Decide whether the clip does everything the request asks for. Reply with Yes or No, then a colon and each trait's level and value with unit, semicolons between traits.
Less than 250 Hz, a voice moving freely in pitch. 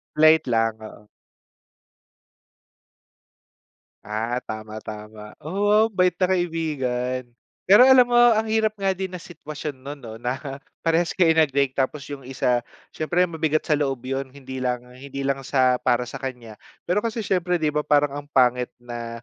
Yes: medium, 140 Hz; wide, 5.9 semitones